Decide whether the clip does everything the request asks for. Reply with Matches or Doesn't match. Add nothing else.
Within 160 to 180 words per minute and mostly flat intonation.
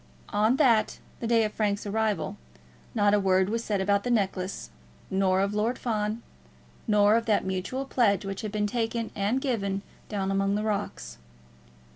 Matches